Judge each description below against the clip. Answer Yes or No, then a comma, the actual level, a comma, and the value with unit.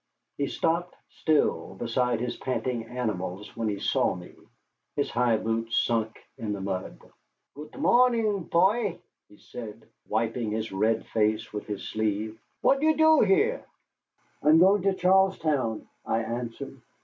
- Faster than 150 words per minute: No, average, 145 wpm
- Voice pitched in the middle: No, low, 120 Hz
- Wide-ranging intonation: Yes, wide, 8.3 semitones